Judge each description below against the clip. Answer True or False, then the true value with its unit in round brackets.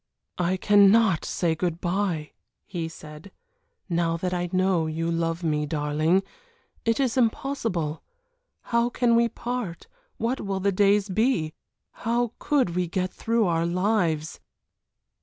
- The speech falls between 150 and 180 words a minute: False (135 wpm)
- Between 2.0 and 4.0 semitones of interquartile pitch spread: False (5.2 semitones)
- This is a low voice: False (185 Hz)